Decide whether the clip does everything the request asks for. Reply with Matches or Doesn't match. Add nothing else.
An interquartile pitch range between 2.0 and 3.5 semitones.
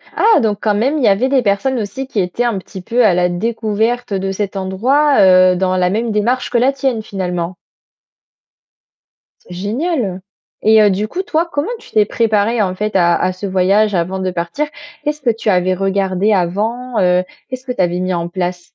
Doesn't match